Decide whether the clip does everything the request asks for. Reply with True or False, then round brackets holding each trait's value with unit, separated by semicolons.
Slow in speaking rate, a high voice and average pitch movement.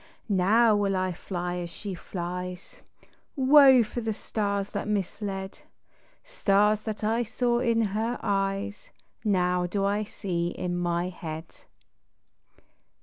True (130 wpm; 200 Hz; 3.3 semitones)